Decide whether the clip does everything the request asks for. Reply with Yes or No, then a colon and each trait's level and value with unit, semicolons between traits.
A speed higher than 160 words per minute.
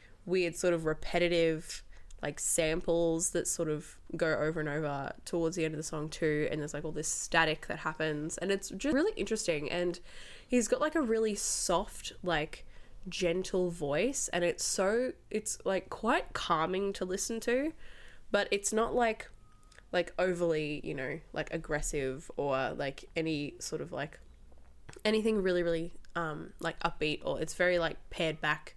Yes: average, 170 wpm